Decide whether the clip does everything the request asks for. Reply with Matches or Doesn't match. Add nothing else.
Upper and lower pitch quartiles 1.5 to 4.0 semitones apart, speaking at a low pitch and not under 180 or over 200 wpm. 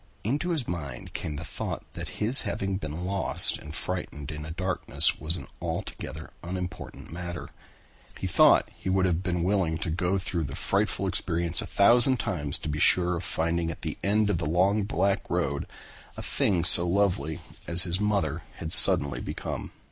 Matches